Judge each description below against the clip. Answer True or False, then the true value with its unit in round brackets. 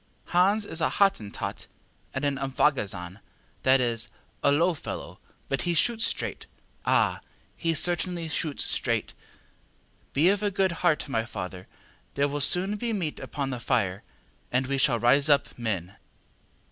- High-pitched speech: False (145 Hz)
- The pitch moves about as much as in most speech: False (6.5 semitones)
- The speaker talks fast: False (150 wpm)